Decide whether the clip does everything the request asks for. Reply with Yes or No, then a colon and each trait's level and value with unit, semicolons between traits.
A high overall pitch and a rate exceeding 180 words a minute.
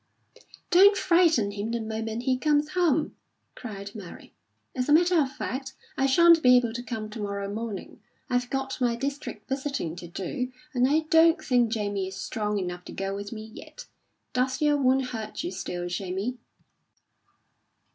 No: high, 245 Hz; average, 170 wpm